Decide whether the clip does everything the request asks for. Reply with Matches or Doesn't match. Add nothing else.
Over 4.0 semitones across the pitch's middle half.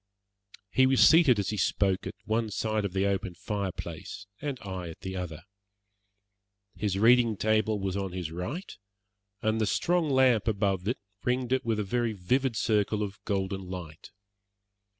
Doesn't match